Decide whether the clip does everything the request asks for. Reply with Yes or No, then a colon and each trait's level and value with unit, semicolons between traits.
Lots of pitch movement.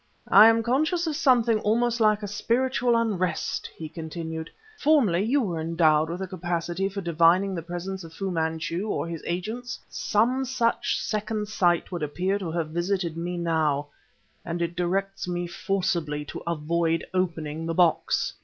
No: average, 4.4 semitones